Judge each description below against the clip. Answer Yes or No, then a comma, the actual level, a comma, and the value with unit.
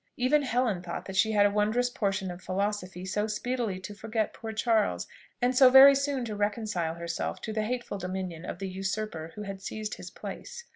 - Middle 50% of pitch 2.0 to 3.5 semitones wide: No, average, 4.0 semitones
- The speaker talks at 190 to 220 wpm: Yes, average, 200 wpm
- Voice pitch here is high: Yes, high, 210 Hz